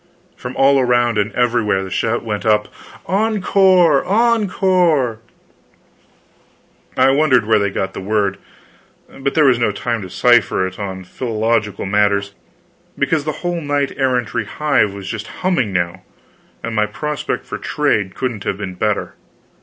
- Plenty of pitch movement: Yes, wide, 5.7 semitones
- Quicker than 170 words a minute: No, average, 145 wpm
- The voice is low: Yes, low, 120 Hz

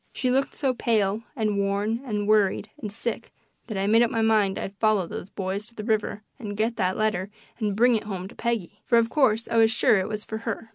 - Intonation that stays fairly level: Yes, narrow, 2.2 semitones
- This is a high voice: Yes, high, 215 Hz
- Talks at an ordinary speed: No, fast, 240 wpm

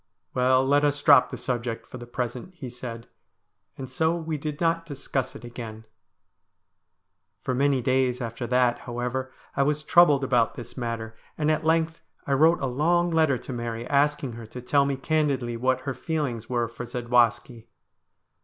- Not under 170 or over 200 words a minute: Yes, average, 175 wpm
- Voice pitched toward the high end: No, low, 130 Hz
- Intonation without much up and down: No, average, 3.4 semitones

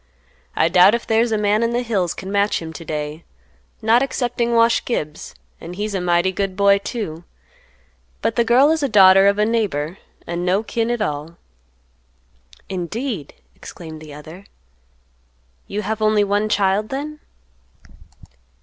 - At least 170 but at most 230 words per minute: No, average, 160 wpm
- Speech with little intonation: No, average, 4.7 semitones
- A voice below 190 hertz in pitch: No, high, 200 Hz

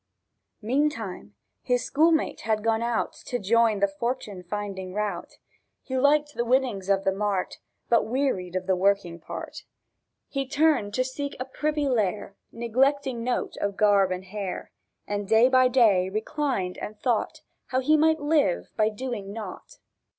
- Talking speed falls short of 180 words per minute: Yes, average, 155 wpm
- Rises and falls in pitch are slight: No, average, 4.8 semitones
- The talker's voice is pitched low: No, high, 225 Hz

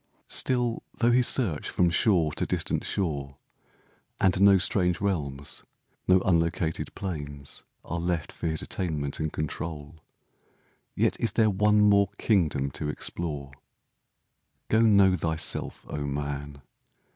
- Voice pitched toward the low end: Yes, very low, 85 Hz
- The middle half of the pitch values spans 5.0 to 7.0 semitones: Yes, average, 5.3 semitones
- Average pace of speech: No, slow, 125 wpm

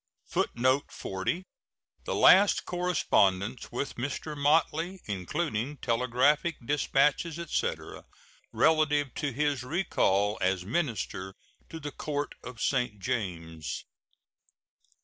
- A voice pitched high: No, low, 135 Hz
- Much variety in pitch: Yes, wide, 6.6 semitones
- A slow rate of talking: Yes, slow, 95 wpm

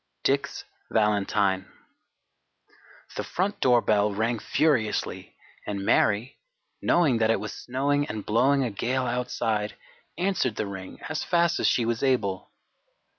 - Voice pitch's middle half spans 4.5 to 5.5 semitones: Yes, average, 4.8 semitones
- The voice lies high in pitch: No, low, 115 Hz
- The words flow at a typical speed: No, slow, 125 wpm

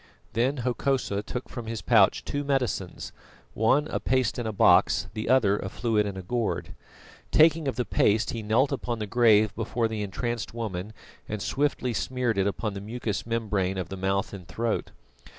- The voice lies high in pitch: No, low, 110 Hz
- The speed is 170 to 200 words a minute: Yes, average, 185 wpm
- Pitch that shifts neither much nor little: Yes, average, 3.4 semitones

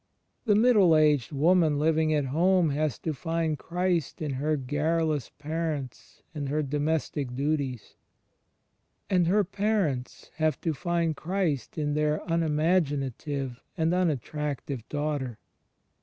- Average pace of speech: No, slow, 120 wpm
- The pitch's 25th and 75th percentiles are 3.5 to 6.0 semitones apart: No, average, 2.7 semitones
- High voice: No, medium, 155 Hz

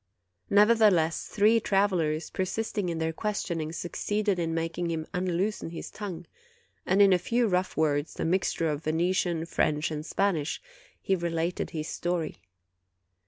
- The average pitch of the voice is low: No, medium, 175 Hz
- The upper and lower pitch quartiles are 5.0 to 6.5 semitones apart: No, average, 3.4 semitones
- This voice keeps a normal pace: Yes, average, 145 wpm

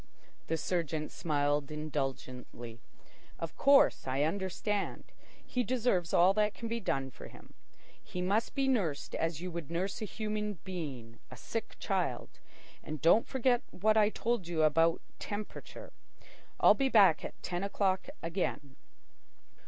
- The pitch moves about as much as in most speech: No, wide, 5.7 semitones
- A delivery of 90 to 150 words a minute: Yes, average, 145 wpm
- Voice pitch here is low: No, medium, 180 Hz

